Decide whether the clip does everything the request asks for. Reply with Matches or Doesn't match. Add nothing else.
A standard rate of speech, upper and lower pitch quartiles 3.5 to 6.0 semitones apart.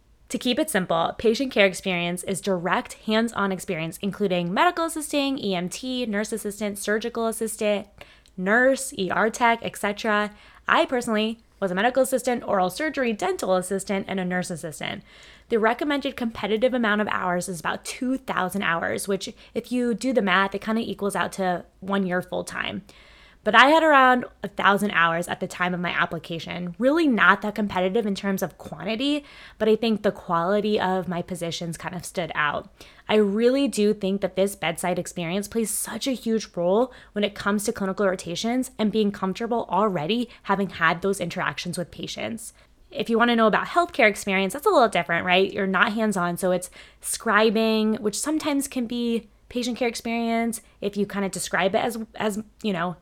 Matches